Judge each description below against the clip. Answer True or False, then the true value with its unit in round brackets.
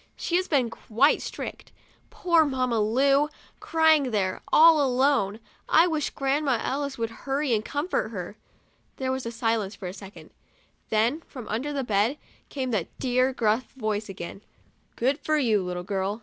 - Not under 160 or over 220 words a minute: True (165 wpm)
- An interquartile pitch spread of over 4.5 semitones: True (4.9 semitones)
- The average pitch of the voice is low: False (250 Hz)